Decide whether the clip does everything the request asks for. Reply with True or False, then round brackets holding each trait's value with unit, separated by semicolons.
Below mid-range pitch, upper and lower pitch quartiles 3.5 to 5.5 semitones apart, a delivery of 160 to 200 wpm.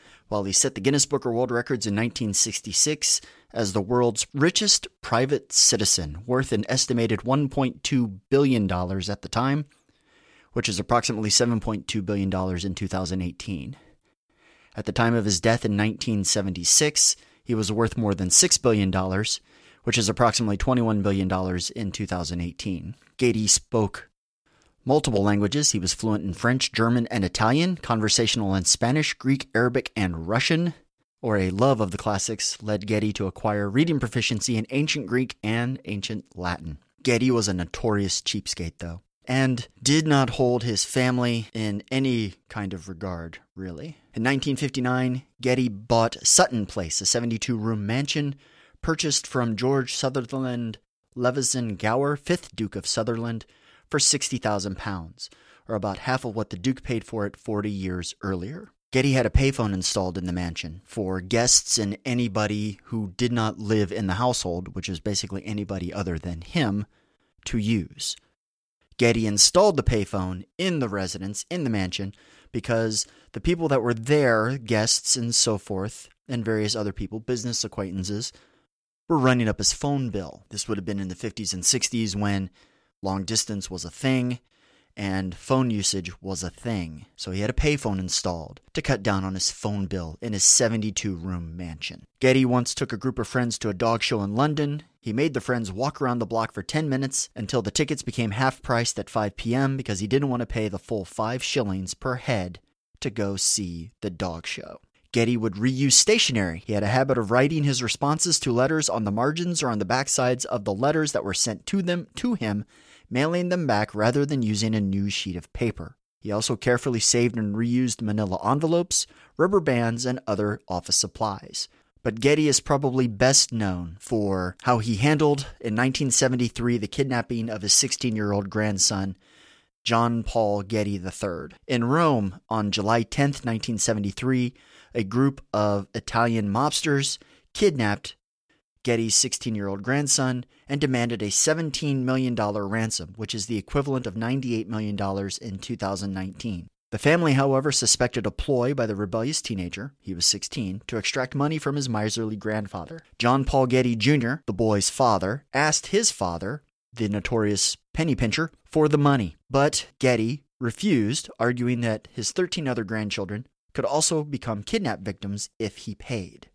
True (115 Hz; 4.3 semitones; 165 wpm)